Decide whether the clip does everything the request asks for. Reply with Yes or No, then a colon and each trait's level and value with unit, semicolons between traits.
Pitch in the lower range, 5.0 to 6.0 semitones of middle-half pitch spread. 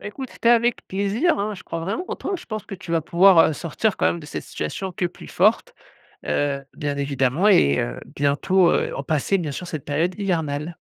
No: medium, 175 Hz; wide, 5.5 semitones